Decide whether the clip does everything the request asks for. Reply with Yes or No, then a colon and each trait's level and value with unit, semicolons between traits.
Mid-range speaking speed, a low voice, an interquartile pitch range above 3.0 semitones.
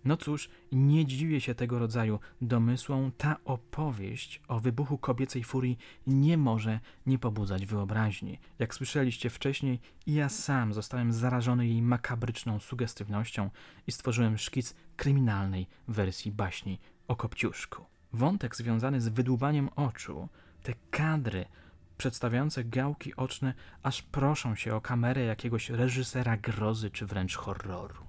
Yes: average, 125 wpm; low, 125 Hz; average, 3.5 semitones